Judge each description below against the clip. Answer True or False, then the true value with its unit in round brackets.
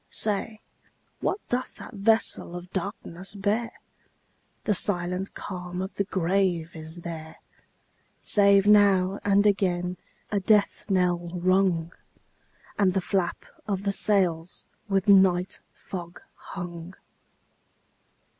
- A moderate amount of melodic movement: False (2.3 semitones)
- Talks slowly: True (110 wpm)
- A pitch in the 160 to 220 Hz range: True (190 Hz)